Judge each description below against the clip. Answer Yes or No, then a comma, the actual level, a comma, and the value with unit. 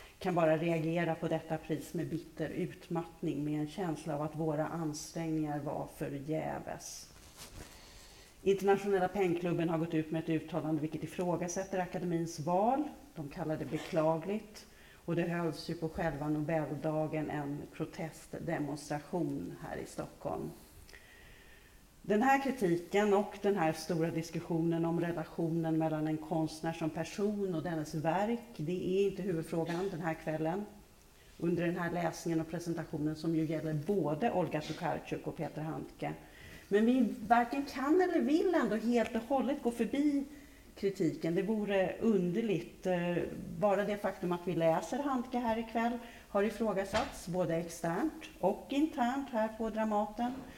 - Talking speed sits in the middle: Yes, average, 145 wpm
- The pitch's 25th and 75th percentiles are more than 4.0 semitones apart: Yes, average, 4.4 semitones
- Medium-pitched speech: Yes, medium, 170 Hz